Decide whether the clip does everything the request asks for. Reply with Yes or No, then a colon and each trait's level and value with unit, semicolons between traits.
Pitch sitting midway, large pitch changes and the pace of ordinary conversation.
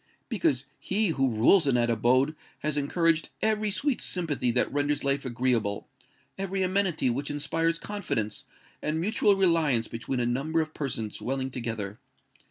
Yes: medium, 145 Hz; wide, 5.9 semitones; average, 145 wpm